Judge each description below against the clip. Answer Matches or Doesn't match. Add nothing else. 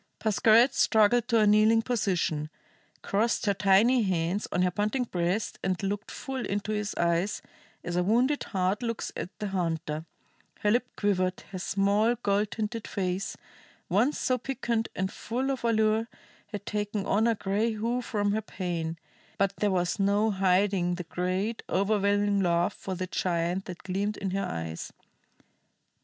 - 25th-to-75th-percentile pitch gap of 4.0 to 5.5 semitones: Doesn't match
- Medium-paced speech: Matches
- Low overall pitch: Doesn't match